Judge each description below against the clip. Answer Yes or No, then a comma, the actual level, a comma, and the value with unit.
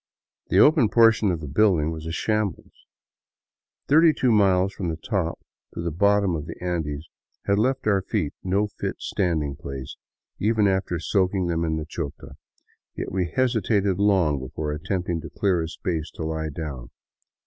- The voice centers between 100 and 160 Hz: No, very low, 90 Hz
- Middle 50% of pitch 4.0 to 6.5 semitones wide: Yes, average, 4.4 semitones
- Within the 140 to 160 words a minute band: No, average, 170 wpm